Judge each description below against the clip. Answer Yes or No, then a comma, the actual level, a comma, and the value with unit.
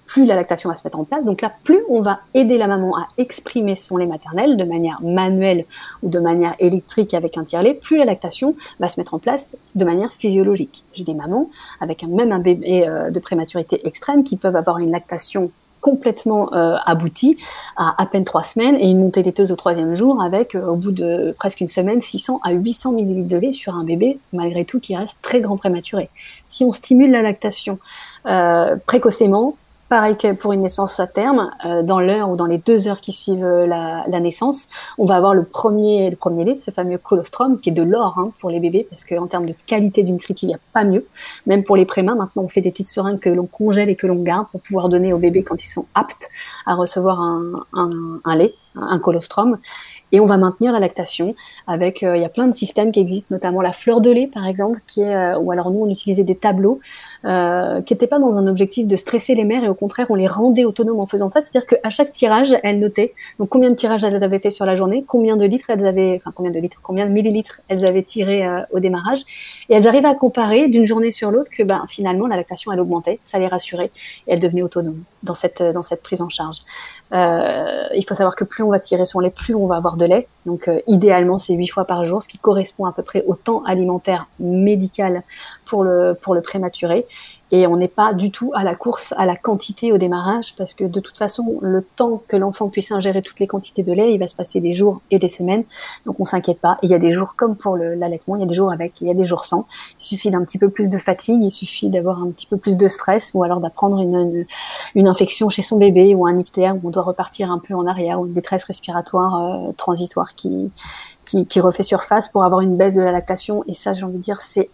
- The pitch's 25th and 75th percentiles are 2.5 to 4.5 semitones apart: Yes, average, 3.3 semitones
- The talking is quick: Yes, fast, 245 wpm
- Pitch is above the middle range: Yes, high, 195 Hz